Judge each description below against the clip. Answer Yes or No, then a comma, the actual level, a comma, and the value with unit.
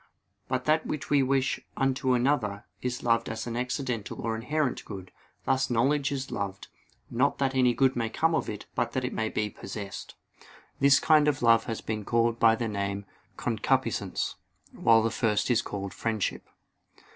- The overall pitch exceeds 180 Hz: No, low, 120 Hz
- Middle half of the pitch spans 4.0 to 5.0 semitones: No, average, 3.3 semitones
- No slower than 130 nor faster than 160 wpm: No, average, 175 wpm